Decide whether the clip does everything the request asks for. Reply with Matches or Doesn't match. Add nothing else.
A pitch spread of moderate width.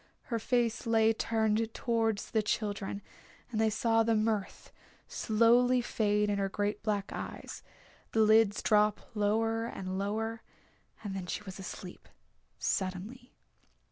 Doesn't match